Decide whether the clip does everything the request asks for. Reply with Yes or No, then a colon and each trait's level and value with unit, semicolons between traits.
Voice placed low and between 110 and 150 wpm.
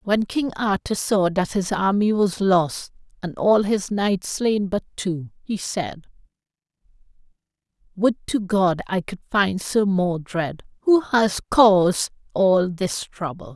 No: high, 195 Hz; average, 140 wpm